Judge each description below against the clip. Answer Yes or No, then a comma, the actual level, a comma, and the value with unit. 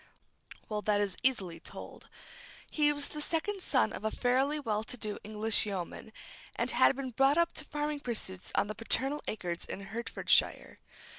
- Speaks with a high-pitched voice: Yes, high, 235 Hz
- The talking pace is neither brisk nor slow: Yes, average, 170 wpm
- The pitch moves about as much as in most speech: No, wide, 5.7 semitones